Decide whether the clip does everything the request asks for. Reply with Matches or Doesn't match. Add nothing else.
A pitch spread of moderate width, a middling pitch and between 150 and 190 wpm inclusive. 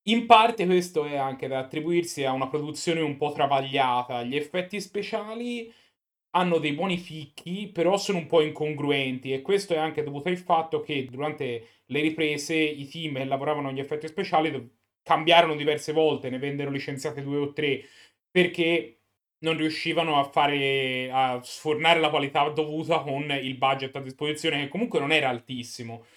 Matches